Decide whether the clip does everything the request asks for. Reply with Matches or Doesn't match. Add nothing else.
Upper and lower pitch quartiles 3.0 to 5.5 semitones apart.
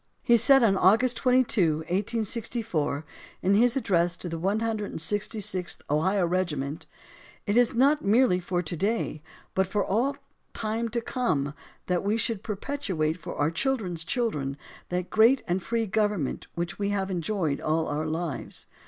Matches